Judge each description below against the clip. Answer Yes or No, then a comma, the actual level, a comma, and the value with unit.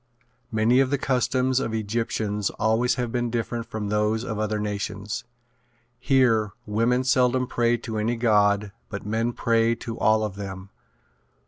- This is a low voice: Yes, low, 115 Hz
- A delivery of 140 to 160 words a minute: Yes, average, 150 wpm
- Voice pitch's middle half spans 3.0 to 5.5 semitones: No, narrow, 2.4 semitones